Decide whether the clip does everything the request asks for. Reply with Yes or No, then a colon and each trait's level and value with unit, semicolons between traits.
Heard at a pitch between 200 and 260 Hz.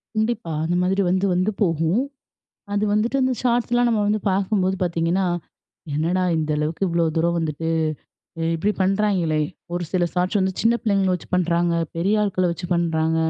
No: medium, 185 Hz